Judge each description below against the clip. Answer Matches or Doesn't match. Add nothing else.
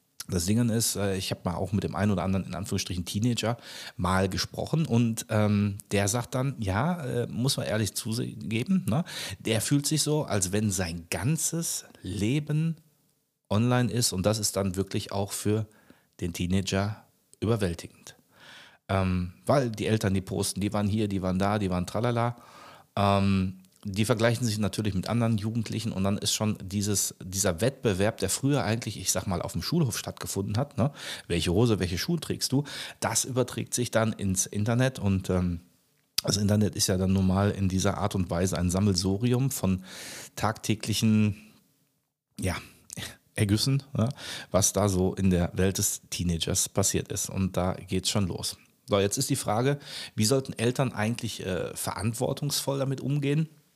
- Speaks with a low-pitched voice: Matches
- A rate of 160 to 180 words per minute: Matches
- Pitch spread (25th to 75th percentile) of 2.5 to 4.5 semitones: Matches